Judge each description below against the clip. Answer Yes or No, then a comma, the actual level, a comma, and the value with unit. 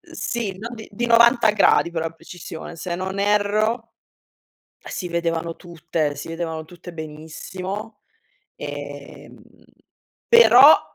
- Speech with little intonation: No, average, 4.7 semitones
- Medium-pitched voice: Yes, medium, 180 Hz